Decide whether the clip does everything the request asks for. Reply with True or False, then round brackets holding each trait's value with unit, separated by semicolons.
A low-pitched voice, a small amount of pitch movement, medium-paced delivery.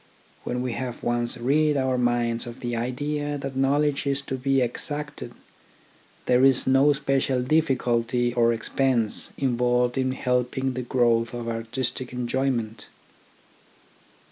False (125 Hz; 2.1 semitones; 130 wpm)